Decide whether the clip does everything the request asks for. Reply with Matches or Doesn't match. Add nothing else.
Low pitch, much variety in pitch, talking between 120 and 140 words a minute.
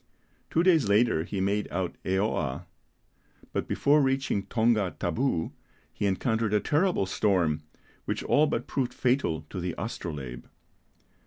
Matches